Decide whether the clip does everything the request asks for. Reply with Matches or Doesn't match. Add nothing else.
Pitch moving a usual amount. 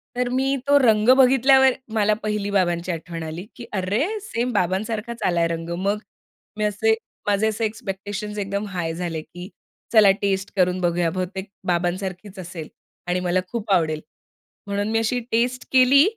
Matches